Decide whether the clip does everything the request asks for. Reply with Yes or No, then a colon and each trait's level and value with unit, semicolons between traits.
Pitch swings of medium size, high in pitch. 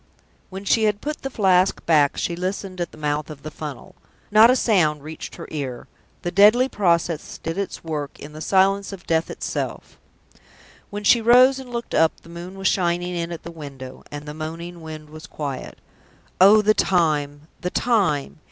No: average, 4.6 semitones; medium, 170 Hz